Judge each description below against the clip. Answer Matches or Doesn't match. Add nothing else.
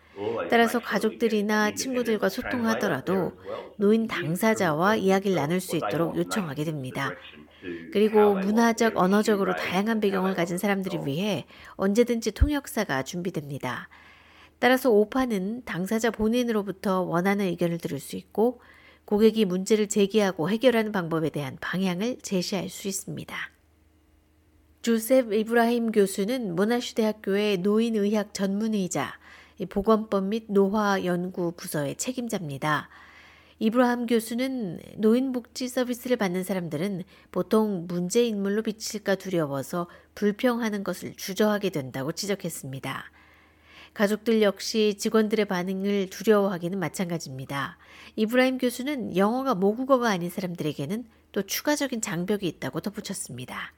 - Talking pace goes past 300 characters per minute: Matches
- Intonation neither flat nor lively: Matches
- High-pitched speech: Matches